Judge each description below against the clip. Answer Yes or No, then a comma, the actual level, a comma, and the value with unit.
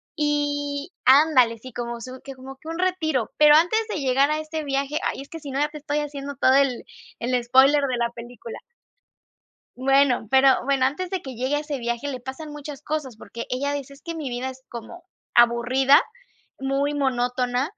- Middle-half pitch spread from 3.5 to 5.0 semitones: No, average, 2.7 semitones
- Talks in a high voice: Yes, very high, 275 Hz